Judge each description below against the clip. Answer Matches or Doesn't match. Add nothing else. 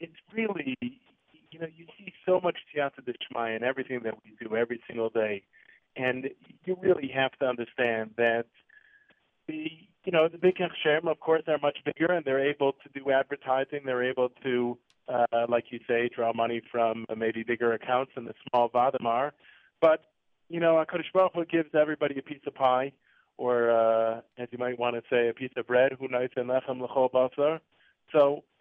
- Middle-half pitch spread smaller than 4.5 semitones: Doesn't match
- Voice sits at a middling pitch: Doesn't match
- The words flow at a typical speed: Matches